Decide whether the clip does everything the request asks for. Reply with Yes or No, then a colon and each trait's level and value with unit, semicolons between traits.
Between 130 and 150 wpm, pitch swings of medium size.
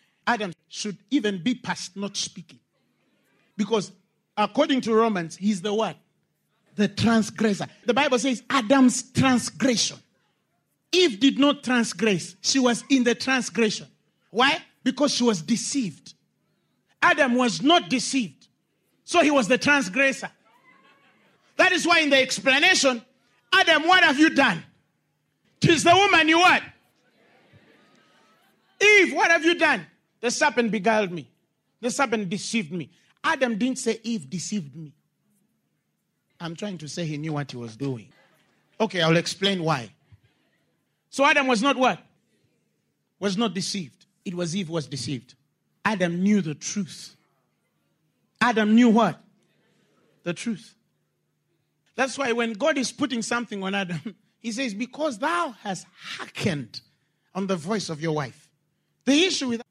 No: average, 140 wpm; wide, 6.7 semitones